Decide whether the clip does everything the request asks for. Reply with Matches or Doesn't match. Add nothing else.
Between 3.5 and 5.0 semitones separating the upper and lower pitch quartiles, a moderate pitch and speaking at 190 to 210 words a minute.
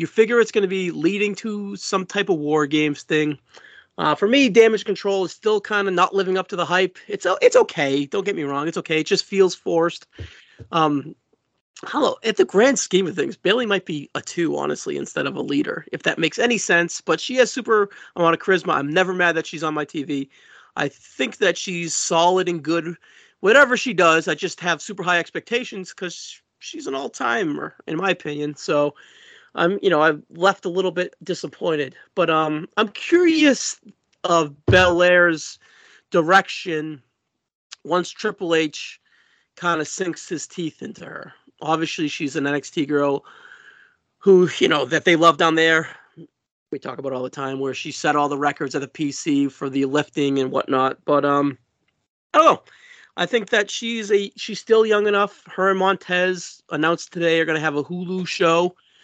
Matches